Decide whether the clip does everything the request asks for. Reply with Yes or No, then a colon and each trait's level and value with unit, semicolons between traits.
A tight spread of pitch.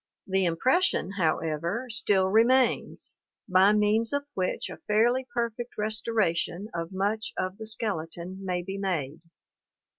No: average, 3.7 semitones